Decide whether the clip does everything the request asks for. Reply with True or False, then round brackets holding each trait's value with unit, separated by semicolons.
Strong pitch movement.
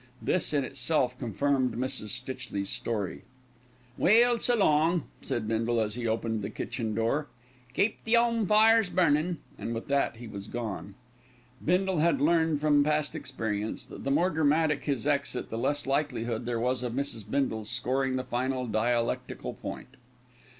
False (4.9 semitones)